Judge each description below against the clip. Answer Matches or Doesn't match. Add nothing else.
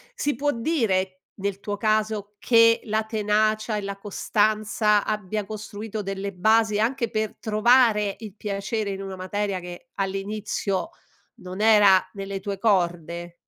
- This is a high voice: Matches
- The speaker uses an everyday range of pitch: Doesn't match